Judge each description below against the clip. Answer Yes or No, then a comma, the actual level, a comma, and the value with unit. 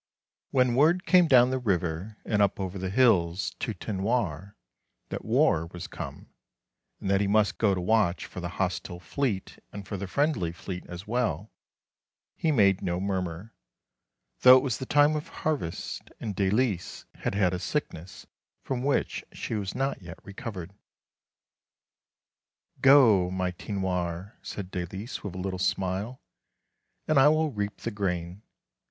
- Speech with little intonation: No, average, 5.2 semitones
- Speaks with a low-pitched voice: Yes, low, 100 Hz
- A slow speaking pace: No, average, 160 wpm